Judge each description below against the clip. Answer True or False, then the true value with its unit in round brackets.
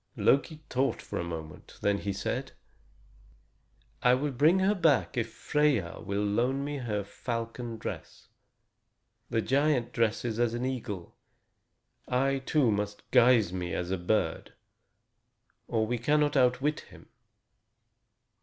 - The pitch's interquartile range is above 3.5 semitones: True (4.8 semitones)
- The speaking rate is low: True (130 wpm)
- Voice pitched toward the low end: True (120 Hz)